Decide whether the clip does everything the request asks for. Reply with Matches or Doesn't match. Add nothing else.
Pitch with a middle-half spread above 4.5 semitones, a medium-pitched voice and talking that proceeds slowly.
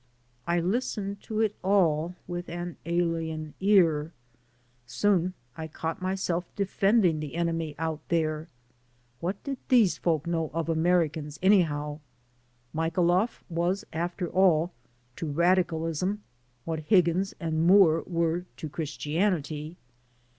Doesn't match